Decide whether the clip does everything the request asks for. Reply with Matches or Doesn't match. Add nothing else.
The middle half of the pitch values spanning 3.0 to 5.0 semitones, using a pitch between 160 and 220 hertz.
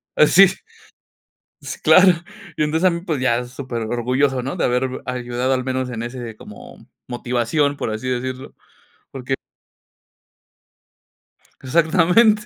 Doesn't match